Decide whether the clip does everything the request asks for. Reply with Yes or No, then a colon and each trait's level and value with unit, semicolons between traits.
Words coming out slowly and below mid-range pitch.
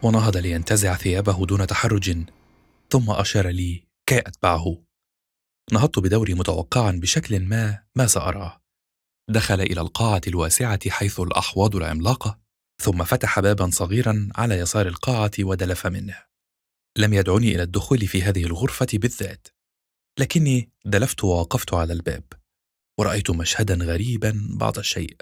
No: average, 120 wpm; low, 100 Hz